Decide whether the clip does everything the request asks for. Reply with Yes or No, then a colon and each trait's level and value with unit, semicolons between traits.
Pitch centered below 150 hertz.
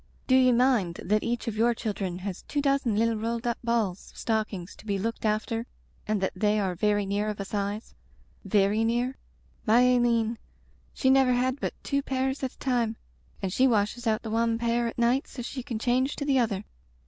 No: high, 230 Hz